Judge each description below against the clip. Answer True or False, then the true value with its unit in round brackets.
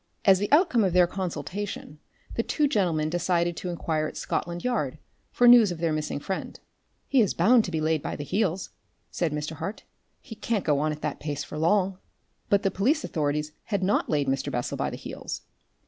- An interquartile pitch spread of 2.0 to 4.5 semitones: False (5.1 semitones)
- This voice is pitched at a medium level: True (175 Hz)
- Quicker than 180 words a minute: True (205 wpm)